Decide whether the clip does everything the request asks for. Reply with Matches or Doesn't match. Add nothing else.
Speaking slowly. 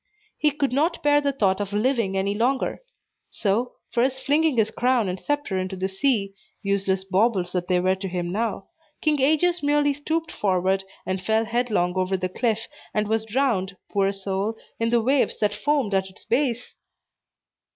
Doesn't match